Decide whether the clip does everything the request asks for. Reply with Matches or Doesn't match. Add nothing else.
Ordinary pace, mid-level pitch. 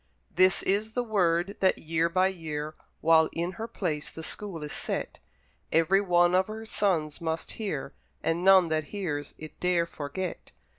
Matches